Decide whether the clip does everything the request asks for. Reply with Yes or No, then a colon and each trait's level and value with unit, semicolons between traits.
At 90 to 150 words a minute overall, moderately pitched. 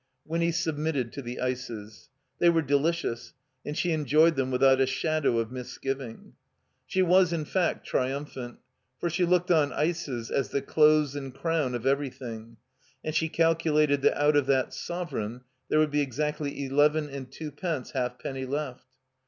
No: average, 165 wpm; medium, 145 Hz